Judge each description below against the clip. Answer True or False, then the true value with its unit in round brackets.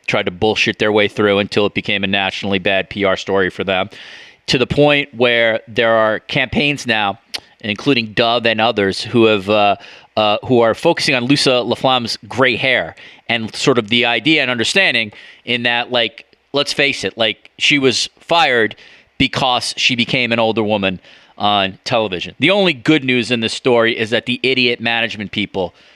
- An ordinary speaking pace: True (180 wpm)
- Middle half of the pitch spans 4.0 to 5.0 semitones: False (3.3 semitones)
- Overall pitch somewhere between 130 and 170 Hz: False (115 Hz)